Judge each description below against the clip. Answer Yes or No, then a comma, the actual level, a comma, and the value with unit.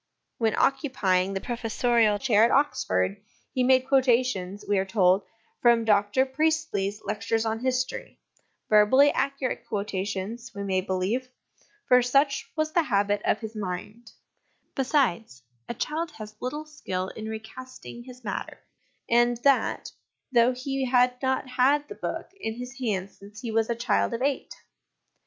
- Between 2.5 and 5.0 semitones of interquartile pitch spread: Yes, average, 4.1 semitones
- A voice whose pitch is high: Yes, high, 235 Hz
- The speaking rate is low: No, average, 145 wpm